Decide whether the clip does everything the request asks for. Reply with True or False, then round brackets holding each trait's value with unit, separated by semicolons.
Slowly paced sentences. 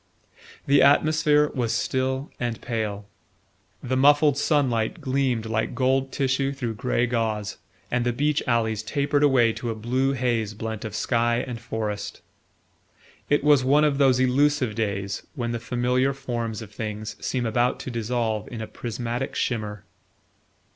False (150 wpm)